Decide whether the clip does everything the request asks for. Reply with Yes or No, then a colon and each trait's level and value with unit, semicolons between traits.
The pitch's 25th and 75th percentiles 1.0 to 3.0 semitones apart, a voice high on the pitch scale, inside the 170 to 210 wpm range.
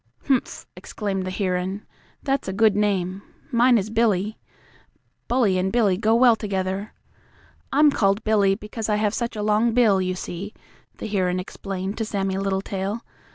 No: average, 2.7 semitones; high, 205 Hz; average, 155 wpm